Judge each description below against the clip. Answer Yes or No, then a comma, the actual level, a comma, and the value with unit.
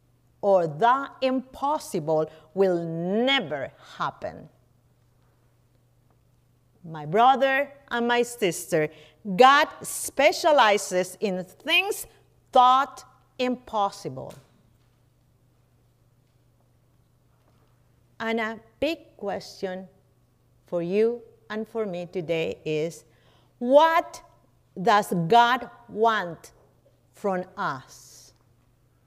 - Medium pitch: Yes, medium, 175 Hz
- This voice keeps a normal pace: No, slow, 70 wpm